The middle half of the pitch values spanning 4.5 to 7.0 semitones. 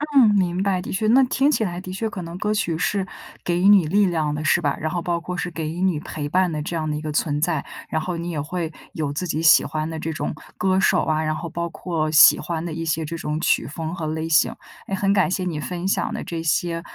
No: average, 2.8 semitones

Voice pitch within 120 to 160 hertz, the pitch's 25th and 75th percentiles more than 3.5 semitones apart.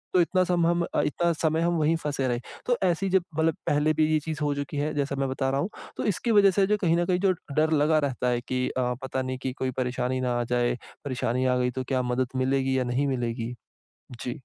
Yes: medium, 140 Hz; average, 4.1 semitones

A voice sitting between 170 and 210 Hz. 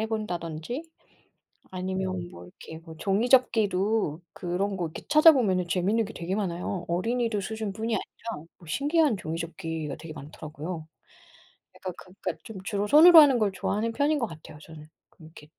Yes: high, 190 Hz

